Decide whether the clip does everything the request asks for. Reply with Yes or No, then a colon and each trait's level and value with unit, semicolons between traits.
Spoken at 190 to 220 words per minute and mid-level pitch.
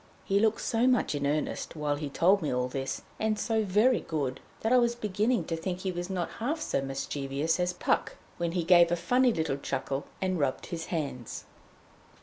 Yes: average, 200 wpm; medium, 175 Hz